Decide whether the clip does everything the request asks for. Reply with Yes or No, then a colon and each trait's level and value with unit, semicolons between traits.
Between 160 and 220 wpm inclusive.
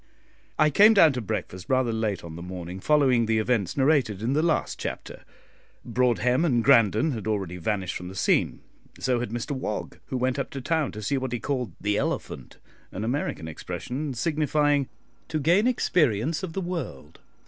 Yes: average, 180 wpm